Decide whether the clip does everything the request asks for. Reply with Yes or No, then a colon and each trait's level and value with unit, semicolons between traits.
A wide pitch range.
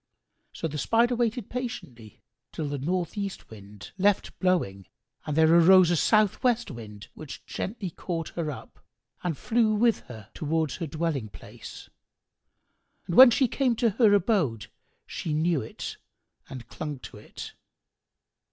Yes: wide, 7.4 semitones